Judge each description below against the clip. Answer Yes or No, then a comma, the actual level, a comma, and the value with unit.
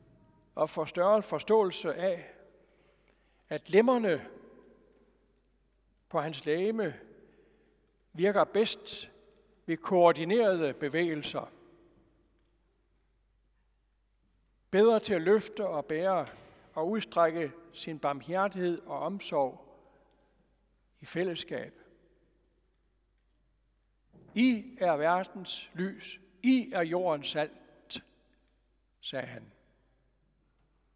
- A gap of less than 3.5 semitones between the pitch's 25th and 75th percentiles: No, average, 4.1 semitones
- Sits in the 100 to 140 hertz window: No, medium, 185 Hz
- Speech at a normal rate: No, slow, 75 wpm